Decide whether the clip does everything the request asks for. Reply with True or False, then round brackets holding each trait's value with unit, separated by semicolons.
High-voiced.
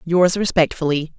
False (170 Hz)